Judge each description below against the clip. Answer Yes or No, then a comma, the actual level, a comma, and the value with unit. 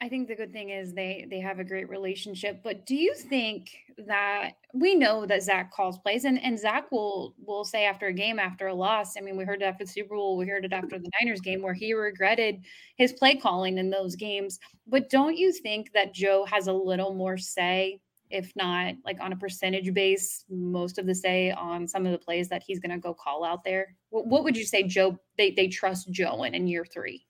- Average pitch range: No, narrow, 2.2 semitones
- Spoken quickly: Yes, fast, 240 wpm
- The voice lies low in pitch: No, high, 195 Hz